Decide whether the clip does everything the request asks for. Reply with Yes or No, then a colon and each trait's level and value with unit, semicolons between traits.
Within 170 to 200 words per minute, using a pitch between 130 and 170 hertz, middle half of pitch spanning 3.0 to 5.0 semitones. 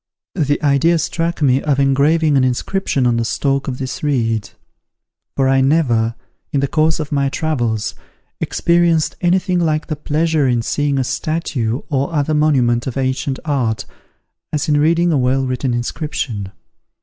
No: average, 160 wpm; medium, 140 Hz; average, 3.5 semitones